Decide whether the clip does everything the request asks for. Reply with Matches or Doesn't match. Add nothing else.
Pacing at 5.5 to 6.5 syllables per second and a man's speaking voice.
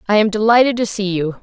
Doesn't match